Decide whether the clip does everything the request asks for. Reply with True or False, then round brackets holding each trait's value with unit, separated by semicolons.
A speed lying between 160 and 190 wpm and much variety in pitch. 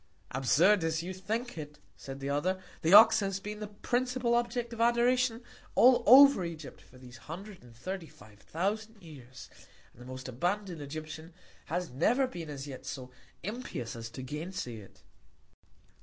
True (170 wpm; 8.1 semitones)